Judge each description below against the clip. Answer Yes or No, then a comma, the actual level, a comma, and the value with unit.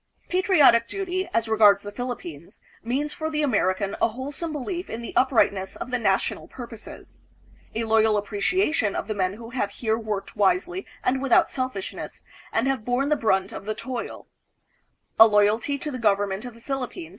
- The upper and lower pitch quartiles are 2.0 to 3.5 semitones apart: No, average, 4.8 semitones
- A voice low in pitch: No, high, 230 Hz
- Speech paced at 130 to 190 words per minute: Yes, average, 180 wpm